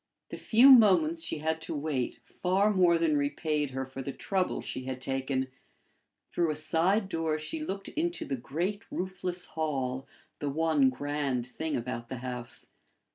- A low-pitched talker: No, medium, 155 Hz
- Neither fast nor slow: Yes, average, 165 wpm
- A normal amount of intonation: No, wide, 5.7 semitones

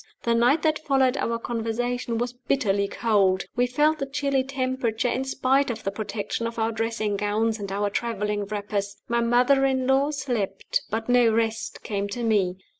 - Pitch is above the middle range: Yes, high, 230 Hz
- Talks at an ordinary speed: Yes, average, 180 wpm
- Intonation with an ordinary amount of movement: Yes, average, 3.6 semitones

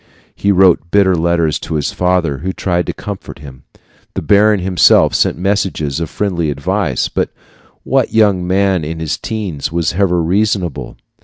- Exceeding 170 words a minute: No, average, 160 wpm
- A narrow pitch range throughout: No, average, 3.4 semitones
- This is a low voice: Yes, very low, 90 Hz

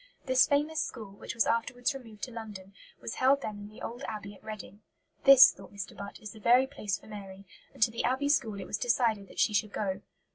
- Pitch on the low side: No, high, 220 Hz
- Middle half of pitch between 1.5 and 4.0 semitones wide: Yes, average, 3.7 semitones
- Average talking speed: No, fast, 230 wpm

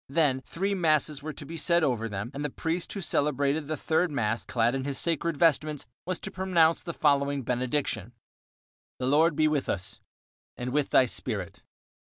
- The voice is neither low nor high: Yes, medium, 145 Hz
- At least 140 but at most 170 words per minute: No, average, 180 wpm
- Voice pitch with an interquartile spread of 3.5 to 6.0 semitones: Yes, average, 4.1 semitones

